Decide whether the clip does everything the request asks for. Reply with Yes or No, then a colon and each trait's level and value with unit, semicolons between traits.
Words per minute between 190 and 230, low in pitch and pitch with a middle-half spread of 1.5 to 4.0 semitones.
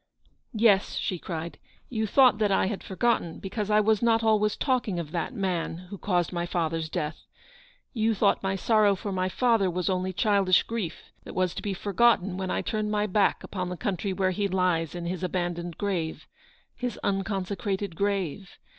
No: average, 200 wpm; high, 195 Hz; average, 2.8 semitones